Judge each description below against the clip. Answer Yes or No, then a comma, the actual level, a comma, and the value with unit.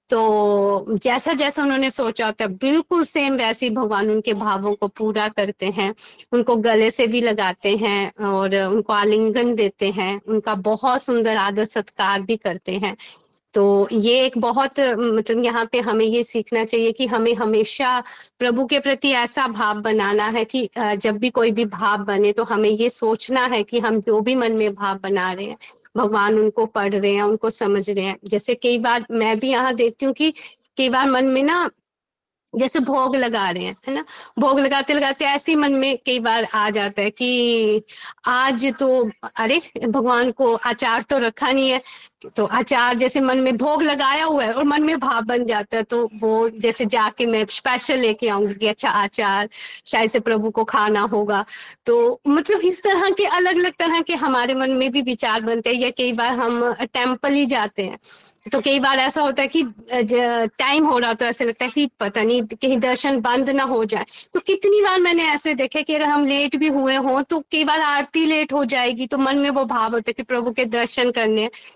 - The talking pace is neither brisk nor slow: No, fast, 205 wpm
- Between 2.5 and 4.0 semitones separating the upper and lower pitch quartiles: Yes, average, 3.7 semitones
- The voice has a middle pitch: No, high, 240 Hz